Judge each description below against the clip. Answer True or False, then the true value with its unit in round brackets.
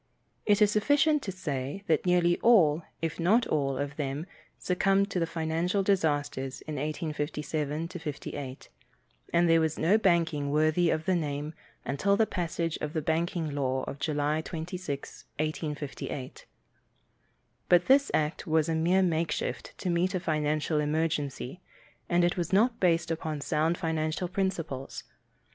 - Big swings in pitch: False (3.1 semitones)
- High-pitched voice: False (160 Hz)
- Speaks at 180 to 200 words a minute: False (145 wpm)